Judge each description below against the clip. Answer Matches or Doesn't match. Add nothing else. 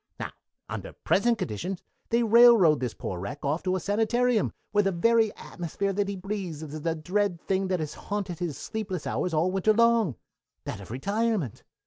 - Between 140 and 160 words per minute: Doesn't match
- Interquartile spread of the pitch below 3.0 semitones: Doesn't match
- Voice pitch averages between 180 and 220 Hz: Matches